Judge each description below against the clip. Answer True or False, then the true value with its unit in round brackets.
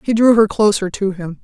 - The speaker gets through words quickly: True (250 wpm)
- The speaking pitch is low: False (205 Hz)